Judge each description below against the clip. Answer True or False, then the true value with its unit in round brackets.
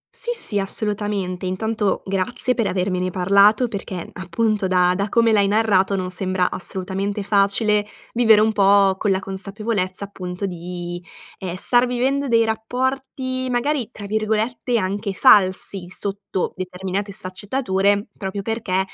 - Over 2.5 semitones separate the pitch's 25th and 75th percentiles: True (2.9 semitones)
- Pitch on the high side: True (200 Hz)